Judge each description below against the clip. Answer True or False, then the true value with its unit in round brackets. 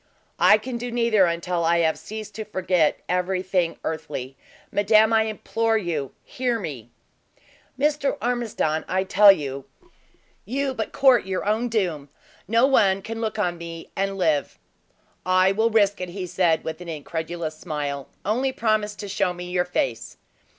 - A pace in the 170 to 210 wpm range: False (160 wpm)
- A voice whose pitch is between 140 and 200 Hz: True (190 Hz)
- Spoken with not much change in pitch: False (4.7 semitones)